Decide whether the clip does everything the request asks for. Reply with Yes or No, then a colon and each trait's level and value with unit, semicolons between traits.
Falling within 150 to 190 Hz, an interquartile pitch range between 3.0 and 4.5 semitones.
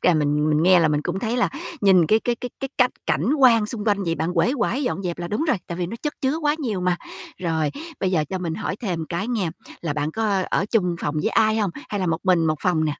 No: medium, 185 Hz; average, 5.3 semitones